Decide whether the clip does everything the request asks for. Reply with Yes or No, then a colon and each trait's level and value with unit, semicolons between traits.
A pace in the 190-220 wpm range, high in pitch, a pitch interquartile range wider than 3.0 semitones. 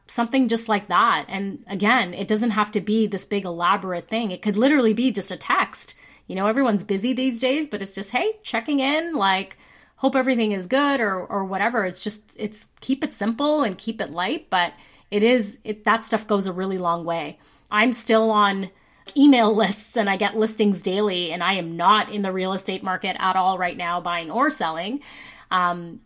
Yes: fast, 205 wpm; high, 210 Hz; average, 3.9 semitones